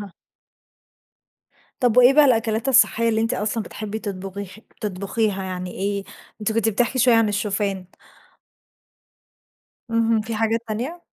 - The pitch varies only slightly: Yes, narrow, 2.3 semitones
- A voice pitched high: Yes, high, 220 Hz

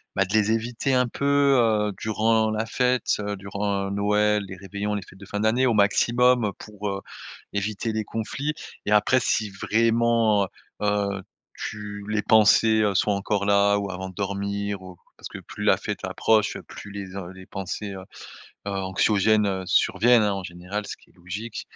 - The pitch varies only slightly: Yes, narrow, 1.9 semitones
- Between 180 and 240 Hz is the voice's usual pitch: No, low, 105 Hz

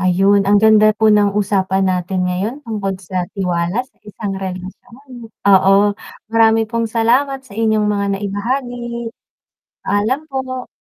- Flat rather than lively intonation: No, average, 3.3 semitones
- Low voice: No, high, 210 Hz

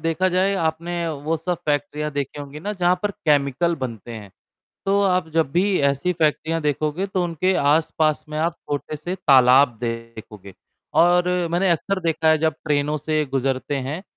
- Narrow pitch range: No, average, 3.6 semitones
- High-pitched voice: No, medium, 155 Hz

